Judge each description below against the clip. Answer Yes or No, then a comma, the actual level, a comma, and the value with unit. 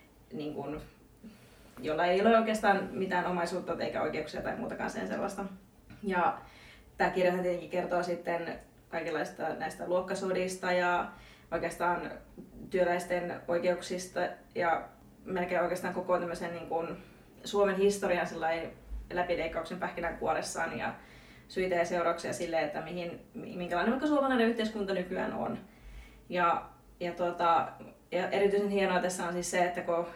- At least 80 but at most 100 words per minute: No, average, 125 wpm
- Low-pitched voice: No, medium, 180 Hz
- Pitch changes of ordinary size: No, narrow, 1.6 semitones